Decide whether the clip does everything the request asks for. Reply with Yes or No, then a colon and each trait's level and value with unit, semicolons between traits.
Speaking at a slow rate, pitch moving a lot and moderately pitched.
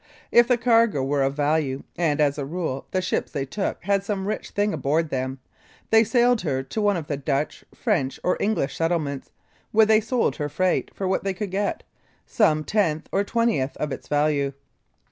No: average, 195 wpm; wide, 6.5 semitones; medium, 170 Hz